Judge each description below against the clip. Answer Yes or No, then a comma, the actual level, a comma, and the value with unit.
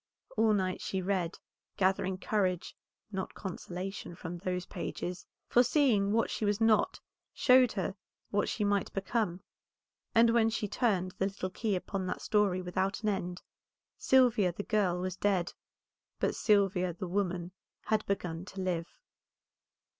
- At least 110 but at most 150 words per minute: Yes, average, 145 wpm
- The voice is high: Yes, high, 195 Hz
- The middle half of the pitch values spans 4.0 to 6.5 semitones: No, average, 2.7 semitones